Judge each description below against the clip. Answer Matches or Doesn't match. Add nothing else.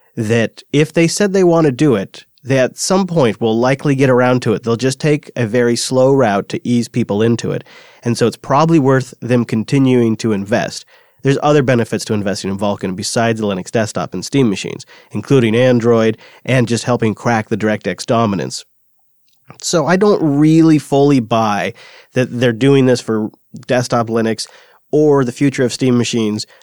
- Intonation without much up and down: Doesn't match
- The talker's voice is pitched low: Matches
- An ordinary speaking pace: Matches